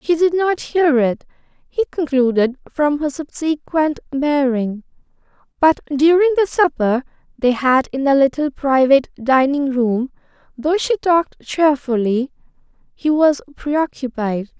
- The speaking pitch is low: No, very high, 285 Hz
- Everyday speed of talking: No, slow, 125 wpm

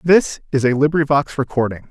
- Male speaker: Yes, male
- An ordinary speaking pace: Yes, average, 155 wpm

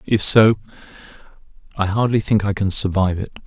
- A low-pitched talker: Yes, low, 100 Hz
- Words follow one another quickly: No, average, 155 wpm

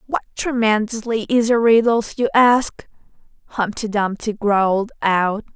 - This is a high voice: Yes, high, 220 Hz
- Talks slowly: Yes, slow, 110 wpm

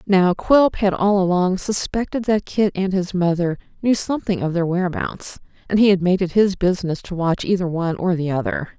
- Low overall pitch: No, medium, 185 Hz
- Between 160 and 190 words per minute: No, fast, 205 wpm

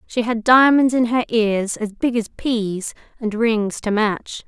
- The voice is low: No, high, 225 Hz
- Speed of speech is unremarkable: Yes, average, 190 wpm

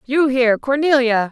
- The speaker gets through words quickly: No, slow, 135 wpm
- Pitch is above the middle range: Yes, very high, 255 Hz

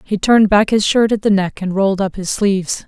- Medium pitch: No, high, 200 Hz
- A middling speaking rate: No, fast, 270 wpm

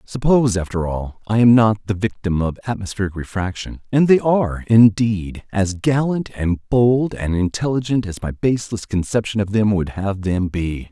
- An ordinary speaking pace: Yes, average, 170 wpm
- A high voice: No, low, 105 Hz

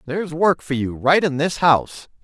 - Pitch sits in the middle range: Yes, medium, 155 Hz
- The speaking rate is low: No, fast, 215 wpm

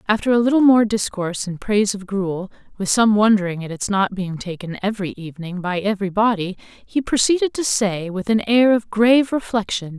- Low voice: No, high, 205 Hz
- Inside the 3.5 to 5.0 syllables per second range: No, 5.5 syllables/s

